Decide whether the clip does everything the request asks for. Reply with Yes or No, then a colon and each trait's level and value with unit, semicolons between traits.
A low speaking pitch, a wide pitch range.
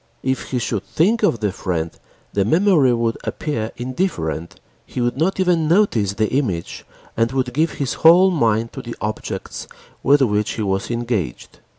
Yes: low, 120 Hz; wide, 6.7 semitones